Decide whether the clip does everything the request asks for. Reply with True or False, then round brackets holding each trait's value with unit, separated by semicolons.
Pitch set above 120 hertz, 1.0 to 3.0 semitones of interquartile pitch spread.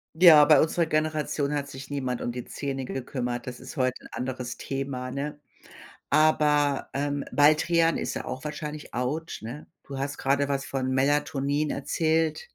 True (140 Hz; 2.5 semitones)